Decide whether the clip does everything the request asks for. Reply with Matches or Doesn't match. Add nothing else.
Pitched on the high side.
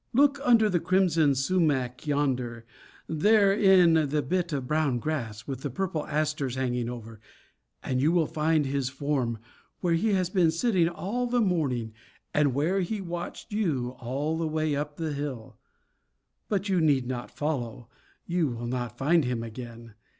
Doesn't match